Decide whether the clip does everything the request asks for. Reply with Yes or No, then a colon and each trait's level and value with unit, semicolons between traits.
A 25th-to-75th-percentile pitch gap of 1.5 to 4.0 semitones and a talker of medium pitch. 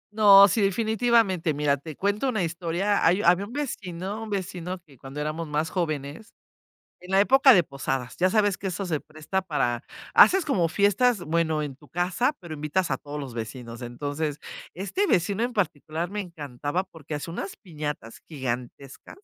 No: average, 5.3 semitones; medium, 170 Hz